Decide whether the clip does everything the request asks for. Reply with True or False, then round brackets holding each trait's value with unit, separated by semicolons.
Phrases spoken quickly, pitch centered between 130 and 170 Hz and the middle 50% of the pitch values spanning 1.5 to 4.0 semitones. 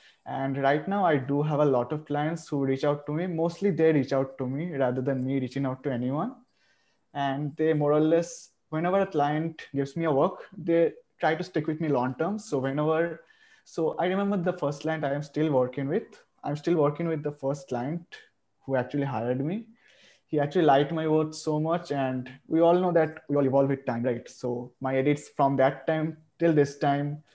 True (215 wpm; 145 Hz; 3.1 semitones)